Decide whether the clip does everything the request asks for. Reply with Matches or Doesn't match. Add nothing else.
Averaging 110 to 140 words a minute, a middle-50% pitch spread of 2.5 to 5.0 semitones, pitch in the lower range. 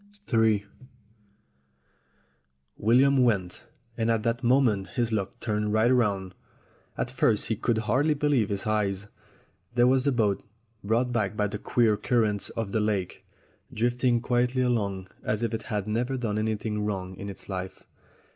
Doesn't match